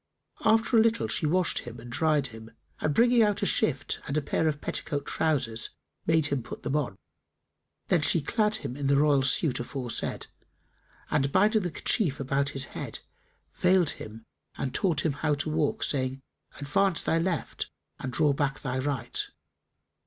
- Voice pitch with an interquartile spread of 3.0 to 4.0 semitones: Yes, average, 3.7 semitones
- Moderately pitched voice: Yes, medium, 145 Hz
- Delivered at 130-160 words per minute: No, average, 175 wpm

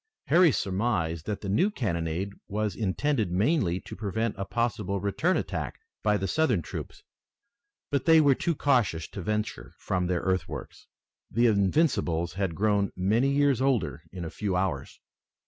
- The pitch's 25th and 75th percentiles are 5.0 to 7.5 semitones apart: Yes, wide, 5.6 semitones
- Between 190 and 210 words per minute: No, average, 155 wpm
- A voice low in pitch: Yes, low, 100 Hz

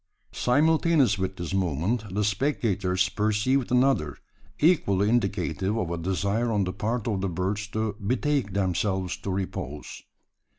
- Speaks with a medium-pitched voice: No, low, 100 Hz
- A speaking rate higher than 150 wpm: No, slow, 135 wpm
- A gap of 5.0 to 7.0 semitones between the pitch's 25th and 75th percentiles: No, average, 4.0 semitones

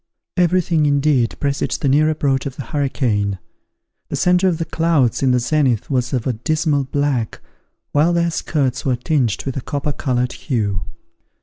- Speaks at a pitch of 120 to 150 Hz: Yes, medium, 140 Hz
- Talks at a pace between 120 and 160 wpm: No, average, 175 wpm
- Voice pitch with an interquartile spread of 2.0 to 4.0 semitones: Yes, average, 3.6 semitones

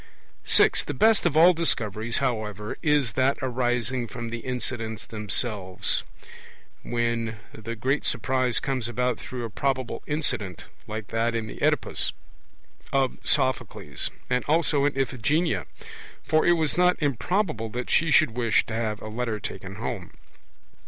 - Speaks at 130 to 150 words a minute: Yes, average, 145 wpm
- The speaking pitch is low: Yes, low, 125 Hz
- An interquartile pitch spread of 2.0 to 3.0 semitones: No, average, 3.7 semitones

